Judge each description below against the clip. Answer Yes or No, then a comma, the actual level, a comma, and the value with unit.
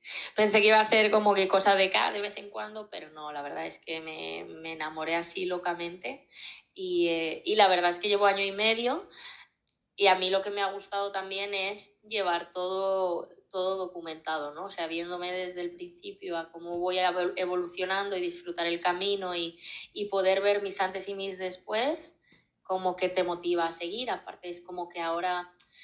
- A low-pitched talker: No, medium, 185 Hz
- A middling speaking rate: No, fast, 200 wpm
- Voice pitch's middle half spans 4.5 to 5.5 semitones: No, narrow, 2.6 semitones